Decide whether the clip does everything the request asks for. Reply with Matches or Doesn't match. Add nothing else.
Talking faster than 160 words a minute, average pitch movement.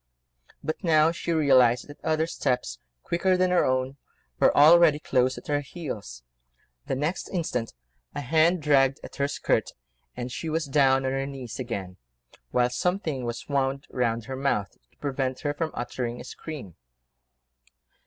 Doesn't match